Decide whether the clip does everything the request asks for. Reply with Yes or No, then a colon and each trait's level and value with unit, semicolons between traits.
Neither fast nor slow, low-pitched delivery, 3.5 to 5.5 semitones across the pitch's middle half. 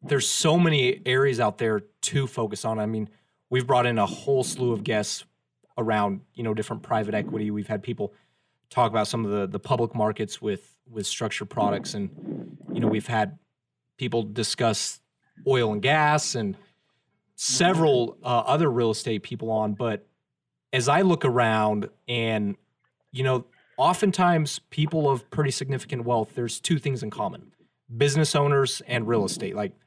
Yes: average, 165 wpm; low, 120 Hz; average, 4.1 semitones